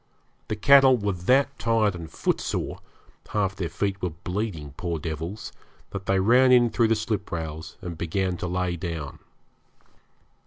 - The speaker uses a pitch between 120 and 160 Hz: No, very low, 95 Hz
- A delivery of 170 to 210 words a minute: No, average, 150 wpm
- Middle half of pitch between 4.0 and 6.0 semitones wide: Yes, average, 4.4 semitones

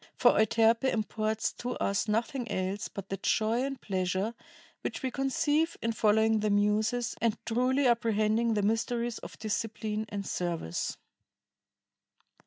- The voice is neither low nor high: No, high, 220 Hz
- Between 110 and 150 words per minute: Yes, slow, 135 wpm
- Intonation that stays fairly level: Yes, narrow, 2.3 semitones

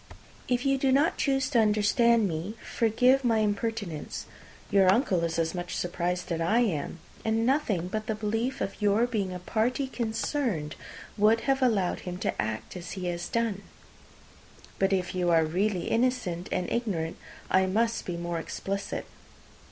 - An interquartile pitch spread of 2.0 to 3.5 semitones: No, average, 4.7 semitones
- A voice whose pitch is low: No, high, 205 Hz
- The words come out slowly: No, average, 165 wpm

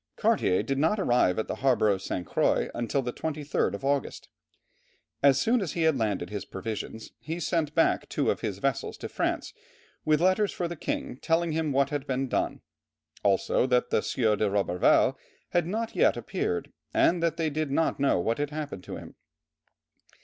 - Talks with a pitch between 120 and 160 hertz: Yes, medium, 140 Hz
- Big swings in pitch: Yes, wide, 6.3 semitones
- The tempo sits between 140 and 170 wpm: No, average, 190 wpm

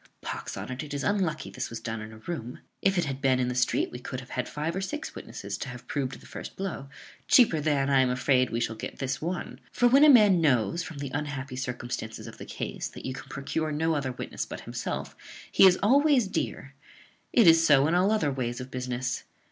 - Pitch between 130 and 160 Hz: Yes, medium, 140 Hz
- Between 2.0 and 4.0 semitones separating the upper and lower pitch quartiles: No, average, 5.3 semitones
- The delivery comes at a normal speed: No, fast, 235 wpm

